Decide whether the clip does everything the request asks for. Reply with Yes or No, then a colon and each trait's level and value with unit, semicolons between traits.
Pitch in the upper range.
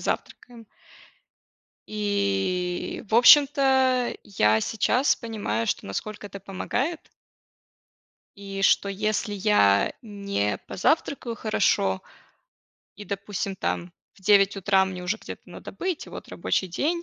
Yes: high, 200 Hz